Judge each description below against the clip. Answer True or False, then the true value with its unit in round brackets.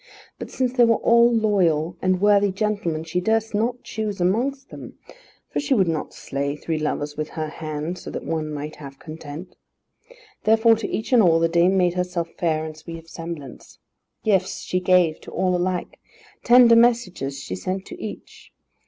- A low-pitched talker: False (180 Hz)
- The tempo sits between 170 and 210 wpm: True (180 wpm)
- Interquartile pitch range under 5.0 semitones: False (5.5 semitones)